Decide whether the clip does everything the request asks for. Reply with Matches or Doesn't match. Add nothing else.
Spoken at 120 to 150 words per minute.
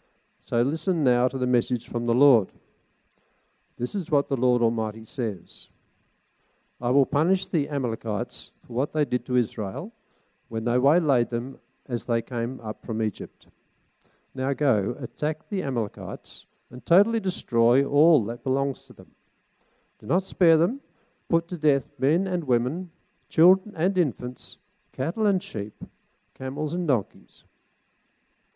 Matches